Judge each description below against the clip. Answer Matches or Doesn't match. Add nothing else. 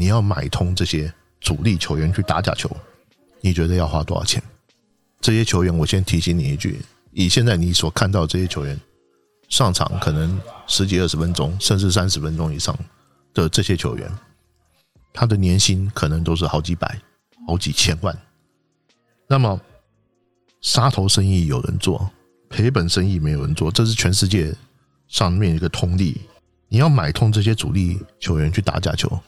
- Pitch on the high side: Doesn't match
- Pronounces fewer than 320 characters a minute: Matches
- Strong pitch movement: Doesn't match